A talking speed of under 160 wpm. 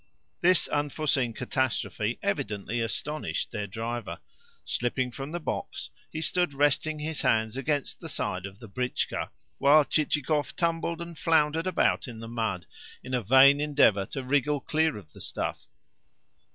Yes: average, 150 wpm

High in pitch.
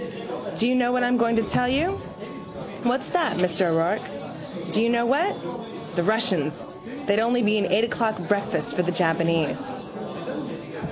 Yes: high, 220 Hz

